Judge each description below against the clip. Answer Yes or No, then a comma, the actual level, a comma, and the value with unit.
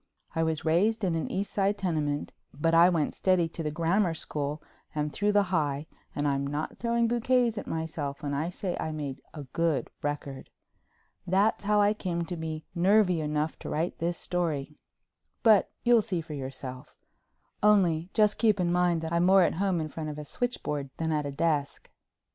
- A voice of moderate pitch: Yes, medium, 165 Hz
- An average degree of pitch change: Yes, average, 4.3 semitones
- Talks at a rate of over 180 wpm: Yes, average, 190 wpm